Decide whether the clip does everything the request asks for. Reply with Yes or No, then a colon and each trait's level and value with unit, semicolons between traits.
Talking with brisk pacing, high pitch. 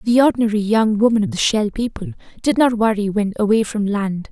Yes: fast, 210 wpm; high, 220 Hz